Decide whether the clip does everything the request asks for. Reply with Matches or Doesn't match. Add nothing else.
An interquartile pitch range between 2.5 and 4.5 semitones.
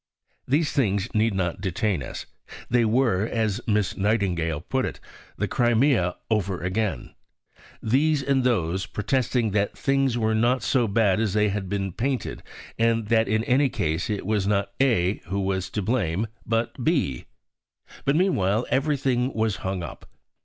Matches